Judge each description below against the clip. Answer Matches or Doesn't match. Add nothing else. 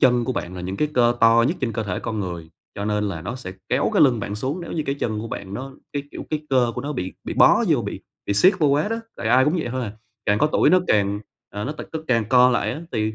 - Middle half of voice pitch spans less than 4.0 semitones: Doesn't match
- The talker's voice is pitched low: Matches